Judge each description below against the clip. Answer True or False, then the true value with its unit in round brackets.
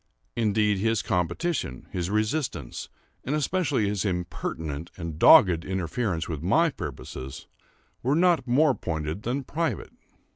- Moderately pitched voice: False (105 Hz)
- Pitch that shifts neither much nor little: False (8.1 semitones)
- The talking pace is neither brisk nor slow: False (120 wpm)